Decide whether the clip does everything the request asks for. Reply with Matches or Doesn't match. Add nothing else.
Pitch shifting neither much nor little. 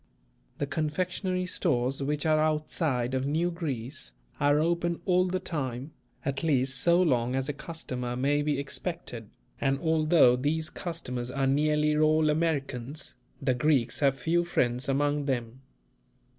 Matches